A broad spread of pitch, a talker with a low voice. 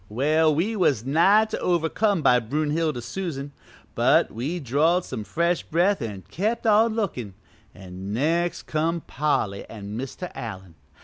No: wide, 6.9 semitones; medium, 155 Hz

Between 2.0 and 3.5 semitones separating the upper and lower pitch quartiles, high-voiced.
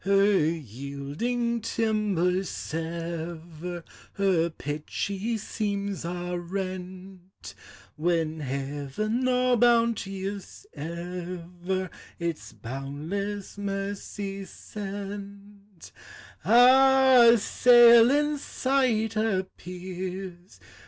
No: average, 4.0 semitones; high, 195 Hz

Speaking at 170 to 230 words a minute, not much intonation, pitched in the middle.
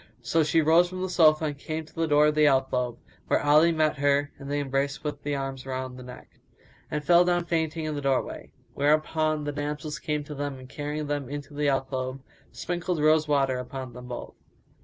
Yes: fast, 205 wpm; narrow, 2.3 semitones; medium, 145 Hz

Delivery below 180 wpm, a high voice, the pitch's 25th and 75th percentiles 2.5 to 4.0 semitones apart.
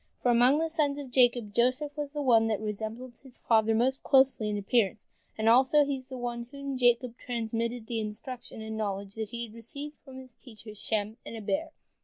No: fast, 205 wpm; high, 240 Hz; average, 3.2 semitones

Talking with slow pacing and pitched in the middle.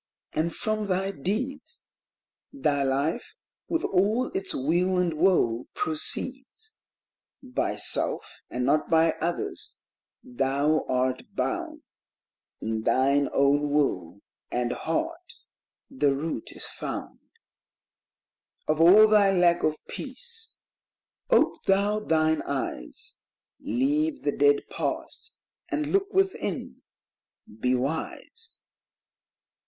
Yes: slow, 105 wpm; medium, 175 Hz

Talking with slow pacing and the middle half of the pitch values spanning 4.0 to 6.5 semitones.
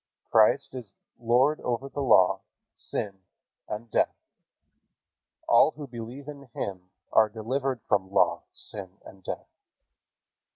Yes: slow, 115 wpm; average, 5.1 semitones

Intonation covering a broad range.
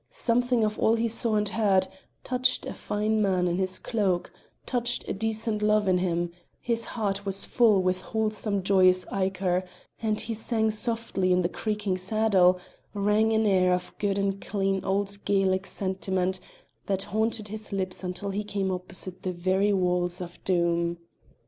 No: average, 2.7 semitones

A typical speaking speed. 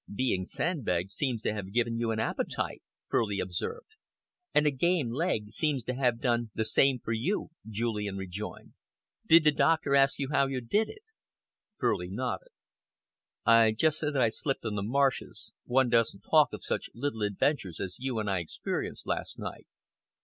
Yes: average, 175 wpm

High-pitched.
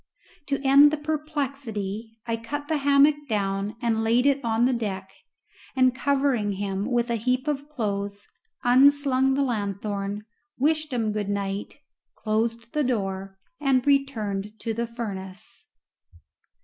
Yes: high, 235 Hz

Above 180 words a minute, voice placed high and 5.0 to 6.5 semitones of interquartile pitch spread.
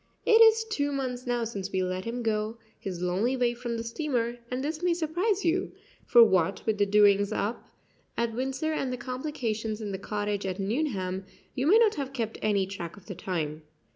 Yes: average, 200 wpm; high, 230 Hz; average, 5.3 semitones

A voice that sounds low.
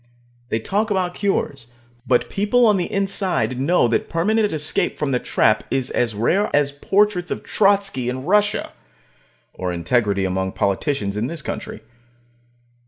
No: medium, 145 Hz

